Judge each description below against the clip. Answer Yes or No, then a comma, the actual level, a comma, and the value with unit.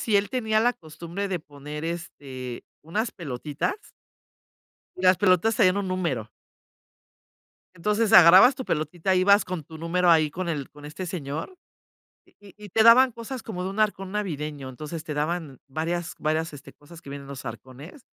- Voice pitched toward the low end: No, medium, 170 Hz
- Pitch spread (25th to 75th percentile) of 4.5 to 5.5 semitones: Yes, average, 5.1 semitones